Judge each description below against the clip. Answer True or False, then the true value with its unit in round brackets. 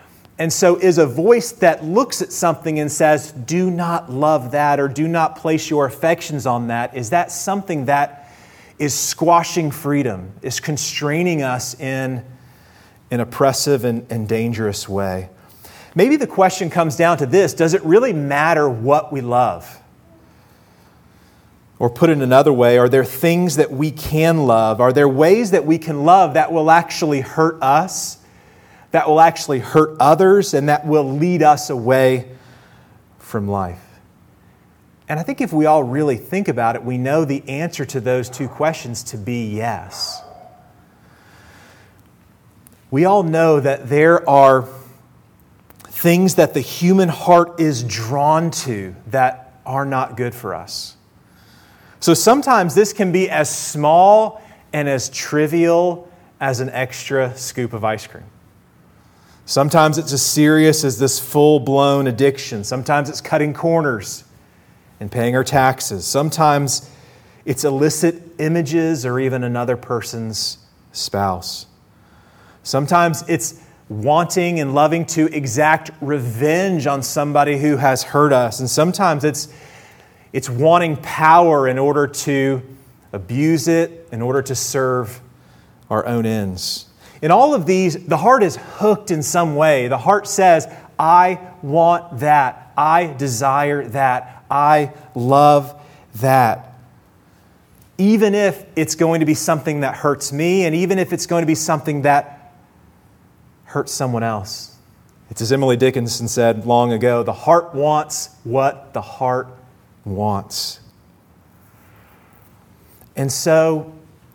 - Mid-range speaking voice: True (145 Hz)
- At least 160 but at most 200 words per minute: False (140 wpm)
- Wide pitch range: False (4.5 semitones)